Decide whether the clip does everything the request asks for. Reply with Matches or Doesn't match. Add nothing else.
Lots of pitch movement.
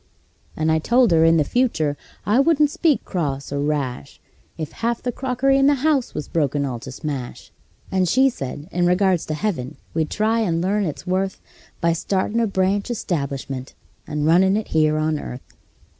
Matches